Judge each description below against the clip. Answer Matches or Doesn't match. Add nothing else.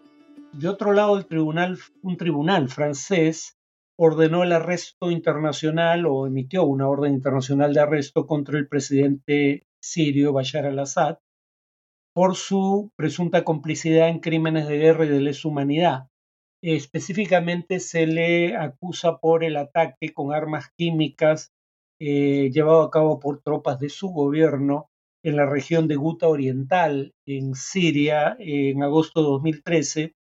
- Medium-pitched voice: Matches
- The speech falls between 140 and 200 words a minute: Doesn't match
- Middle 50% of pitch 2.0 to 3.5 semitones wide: Matches